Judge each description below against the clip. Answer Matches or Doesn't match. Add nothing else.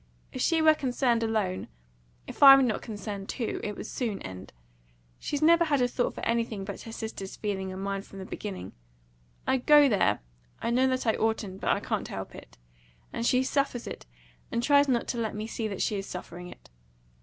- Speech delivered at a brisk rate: Matches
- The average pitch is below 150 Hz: Doesn't match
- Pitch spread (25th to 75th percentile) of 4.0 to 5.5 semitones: Matches